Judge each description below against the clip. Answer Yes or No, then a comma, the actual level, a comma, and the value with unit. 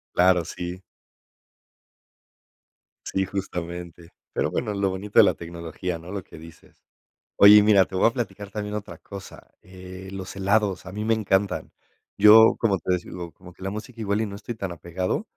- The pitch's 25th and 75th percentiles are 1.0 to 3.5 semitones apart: Yes, average, 2.7 semitones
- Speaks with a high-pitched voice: No, very low, 95 Hz